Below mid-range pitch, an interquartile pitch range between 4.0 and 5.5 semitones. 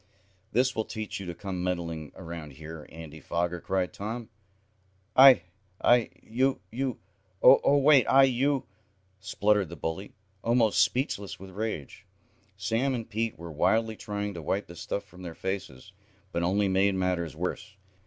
Yes: low, 100 Hz; average, 4.8 semitones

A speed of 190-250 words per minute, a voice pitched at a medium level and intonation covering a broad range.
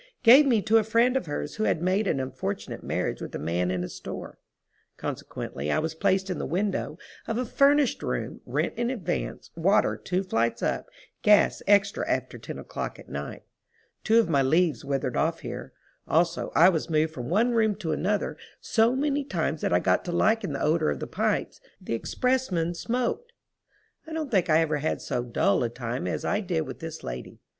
Yes: average, 200 wpm; medium, 175 Hz; wide, 8.0 semitones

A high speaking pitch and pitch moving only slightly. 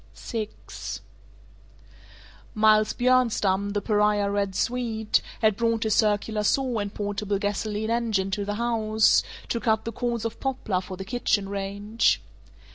Yes: high, 215 Hz; narrow, 2.1 semitones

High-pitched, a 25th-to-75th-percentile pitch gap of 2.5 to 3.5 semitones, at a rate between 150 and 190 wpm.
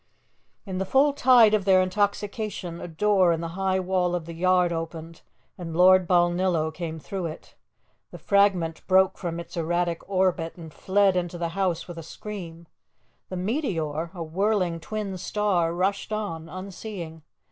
No: medium, 180 Hz; average, 2.9 semitones; average, 160 wpm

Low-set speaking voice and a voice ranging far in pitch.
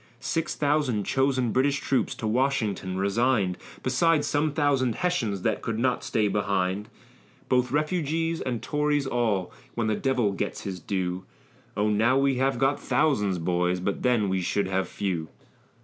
Yes: low, 120 Hz; wide, 5.8 semitones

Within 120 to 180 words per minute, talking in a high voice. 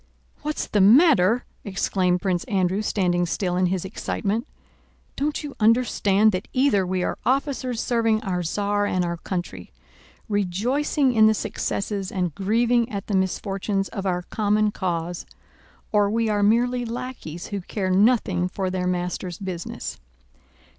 Yes: average, 145 wpm; high, 200 Hz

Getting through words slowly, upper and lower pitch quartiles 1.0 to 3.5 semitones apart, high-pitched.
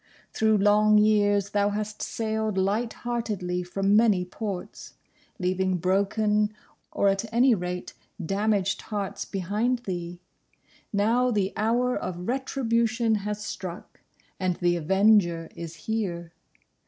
Yes: slow, 115 wpm; average, 2.9 semitones; high, 205 Hz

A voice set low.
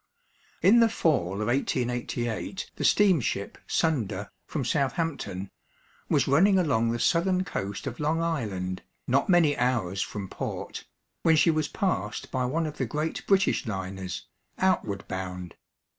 Yes: low, 130 Hz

